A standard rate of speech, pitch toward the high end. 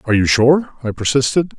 No: average, 190 wpm; low, 130 Hz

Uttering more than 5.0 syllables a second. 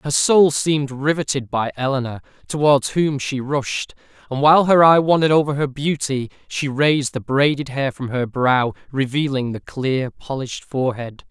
No: 4.9 syllables/s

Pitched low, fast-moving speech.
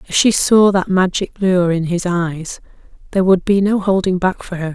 No: medium, 185 Hz; fast, 215 wpm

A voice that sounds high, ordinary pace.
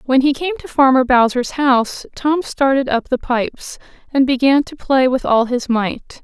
Yes: very high, 265 Hz; average, 195 wpm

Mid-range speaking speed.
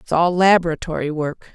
Yes: average, 155 wpm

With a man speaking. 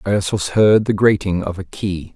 Yes: male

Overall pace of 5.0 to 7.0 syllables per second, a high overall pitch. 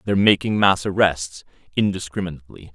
No: 6.1 syllables/s; very low, 95 Hz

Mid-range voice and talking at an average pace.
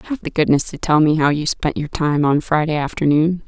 No: medium, 155 Hz; fast, 240 wpm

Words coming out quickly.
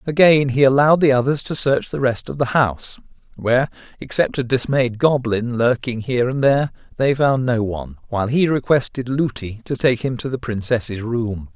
No: average, 175 wpm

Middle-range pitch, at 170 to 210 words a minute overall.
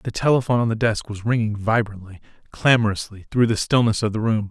No: low, 110 Hz; average, 200 wpm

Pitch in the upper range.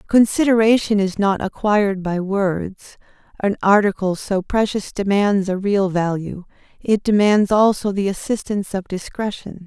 Yes: high, 200 Hz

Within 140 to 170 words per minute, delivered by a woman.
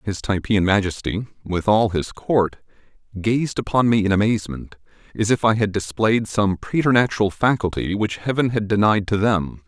No: average, 160 wpm; male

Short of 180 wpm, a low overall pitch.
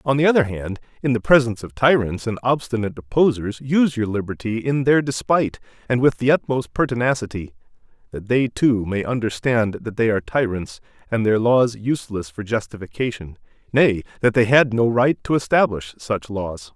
Yes: average, 170 wpm; low, 115 Hz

